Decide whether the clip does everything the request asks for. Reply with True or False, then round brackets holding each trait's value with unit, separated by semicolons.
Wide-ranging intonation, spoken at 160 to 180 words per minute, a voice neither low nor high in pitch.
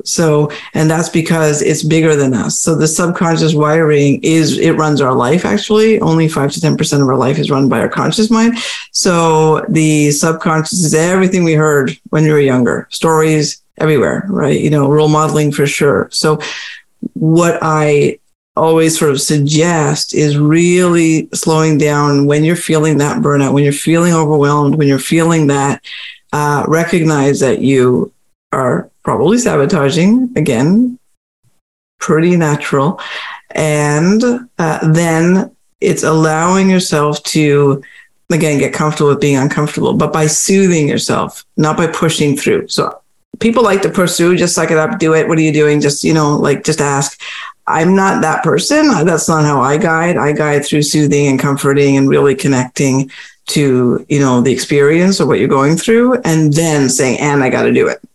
False (2.7 semitones; 170 wpm; 155 Hz)